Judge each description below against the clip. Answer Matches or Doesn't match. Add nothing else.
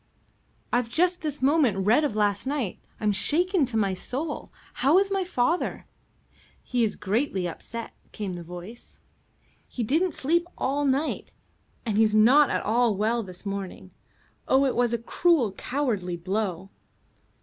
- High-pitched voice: Matches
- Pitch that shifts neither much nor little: Doesn't match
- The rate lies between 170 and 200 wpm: Doesn't match